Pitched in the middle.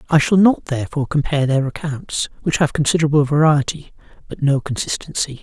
Yes: medium, 145 Hz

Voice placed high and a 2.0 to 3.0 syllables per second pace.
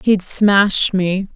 Yes: high, 195 Hz; 2.5 syllables/s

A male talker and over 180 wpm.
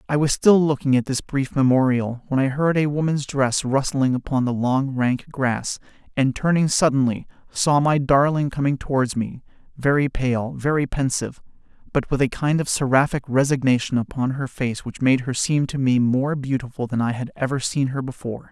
Yes: male; average, 190 wpm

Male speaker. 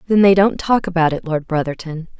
No: female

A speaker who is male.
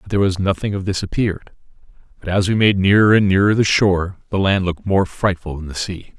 Yes: male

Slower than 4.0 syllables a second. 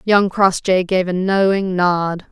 Yes: 3.6 syllables/s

